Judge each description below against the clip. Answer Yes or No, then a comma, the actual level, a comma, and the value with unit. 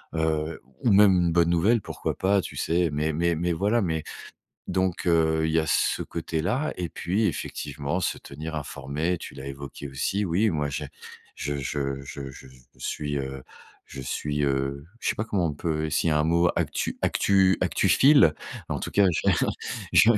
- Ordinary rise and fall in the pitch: Yes, average, 3.7 semitones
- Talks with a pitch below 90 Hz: Yes, very low, 80 Hz